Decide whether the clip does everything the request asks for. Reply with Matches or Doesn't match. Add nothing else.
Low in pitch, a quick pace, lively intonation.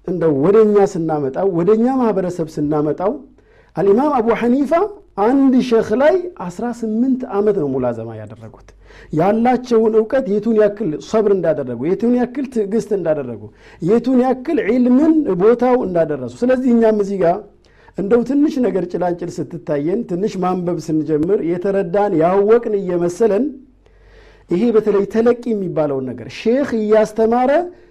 Doesn't match